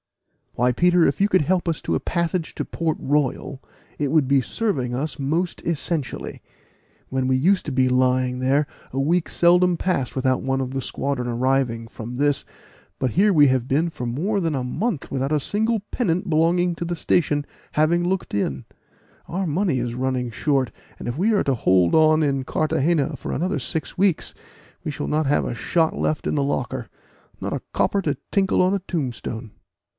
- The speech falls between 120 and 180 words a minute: No, average, 190 wpm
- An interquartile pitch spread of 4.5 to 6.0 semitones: Yes, average, 5.0 semitones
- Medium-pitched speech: Yes, medium, 145 Hz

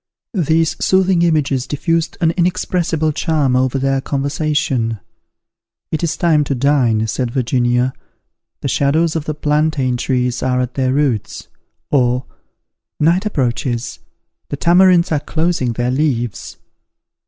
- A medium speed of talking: No, slow, 125 wpm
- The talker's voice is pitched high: No, medium, 140 Hz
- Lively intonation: No, average, 4.2 semitones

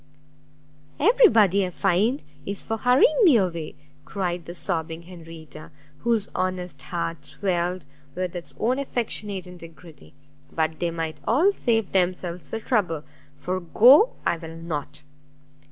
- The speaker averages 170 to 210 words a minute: No, slow, 135 wpm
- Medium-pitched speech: Yes, medium, 180 Hz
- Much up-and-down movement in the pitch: No, average, 4.9 semitones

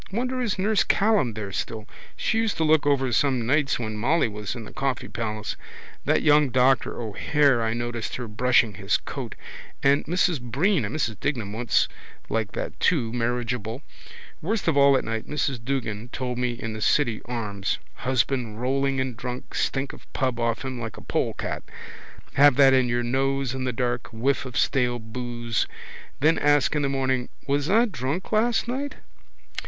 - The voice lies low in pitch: Yes, low, 130 Hz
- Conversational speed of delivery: Yes, average, 180 wpm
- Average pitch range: Yes, average, 3.6 semitones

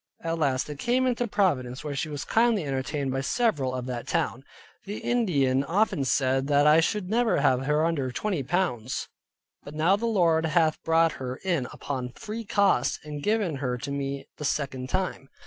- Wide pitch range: Yes, wide, 6.1 semitones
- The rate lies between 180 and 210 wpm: Yes, average, 185 wpm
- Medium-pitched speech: Yes, medium, 150 Hz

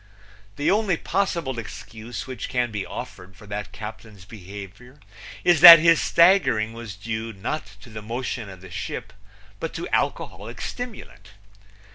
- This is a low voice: Yes, low, 115 Hz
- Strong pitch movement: Yes, wide, 7.0 semitones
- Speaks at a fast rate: No, average, 145 wpm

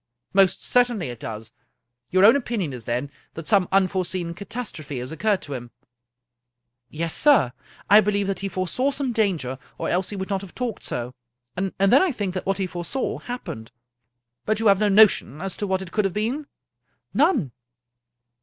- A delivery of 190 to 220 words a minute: Yes, average, 200 wpm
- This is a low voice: No, high, 190 Hz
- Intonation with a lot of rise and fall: Yes, wide, 7.2 semitones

